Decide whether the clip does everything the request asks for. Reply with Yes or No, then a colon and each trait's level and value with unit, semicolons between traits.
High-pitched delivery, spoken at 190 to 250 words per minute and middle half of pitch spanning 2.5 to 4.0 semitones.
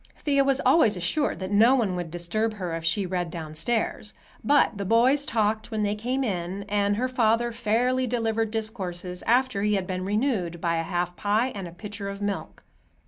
No: high, 210 Hz; average, 195 wpm; average, 4.4 semitones